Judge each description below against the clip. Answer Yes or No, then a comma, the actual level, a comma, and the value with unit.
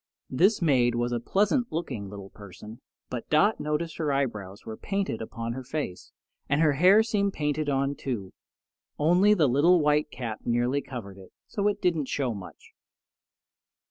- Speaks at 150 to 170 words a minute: Yes, average, 165 wpm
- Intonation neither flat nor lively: No, wide, 6.2 semitones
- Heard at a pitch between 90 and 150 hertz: Yes, medium, 140 Hz